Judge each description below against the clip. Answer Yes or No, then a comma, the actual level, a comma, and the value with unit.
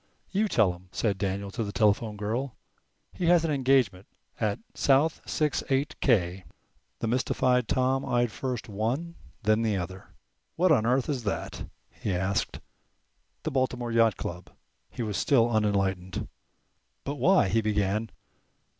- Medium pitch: No, low, 115 Hz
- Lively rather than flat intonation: No, average, 4.8 semitones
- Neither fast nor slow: Yes, average, 145 wpm